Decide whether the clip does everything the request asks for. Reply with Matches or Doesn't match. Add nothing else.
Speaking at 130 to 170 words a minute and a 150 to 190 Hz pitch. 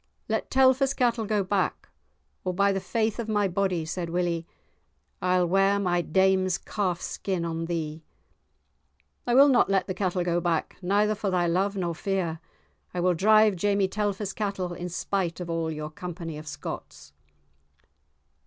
Matches